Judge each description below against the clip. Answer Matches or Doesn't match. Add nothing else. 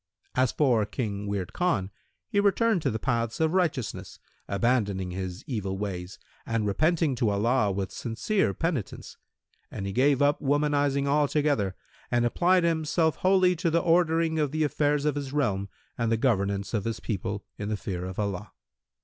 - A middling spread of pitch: Doesn't match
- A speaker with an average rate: Matches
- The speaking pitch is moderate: Doesn't match